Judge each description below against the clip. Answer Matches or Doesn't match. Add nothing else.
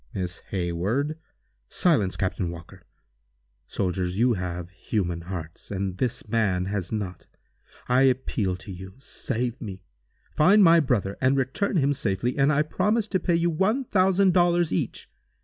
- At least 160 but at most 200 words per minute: Doesn't match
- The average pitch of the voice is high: Doesn't match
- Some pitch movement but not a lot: Doesn't match